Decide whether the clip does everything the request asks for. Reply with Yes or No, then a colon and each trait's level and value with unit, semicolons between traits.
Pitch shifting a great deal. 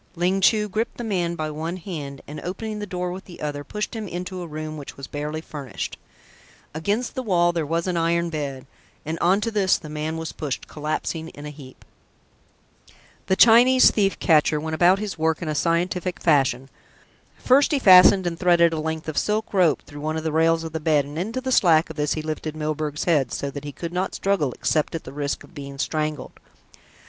No: average, 3.5 semitones